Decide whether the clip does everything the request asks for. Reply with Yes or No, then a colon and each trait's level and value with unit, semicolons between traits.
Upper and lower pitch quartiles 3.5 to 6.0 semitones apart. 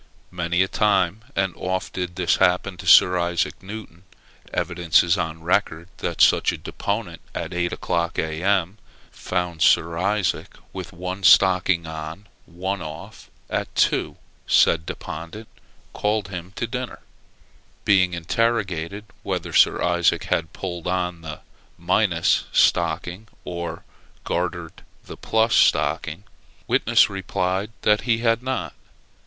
No: average, 2.8 semitones